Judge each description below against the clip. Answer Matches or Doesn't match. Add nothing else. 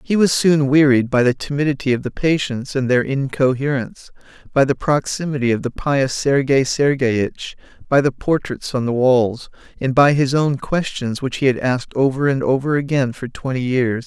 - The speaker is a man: Matches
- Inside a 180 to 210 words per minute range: Matches